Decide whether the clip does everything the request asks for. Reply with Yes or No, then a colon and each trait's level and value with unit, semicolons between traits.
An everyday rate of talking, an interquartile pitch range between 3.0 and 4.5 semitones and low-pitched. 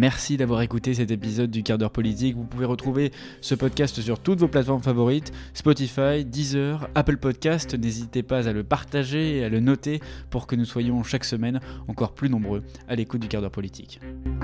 Yes: average, 195 wpm; average, 3.4 semitones; low, 125 Hz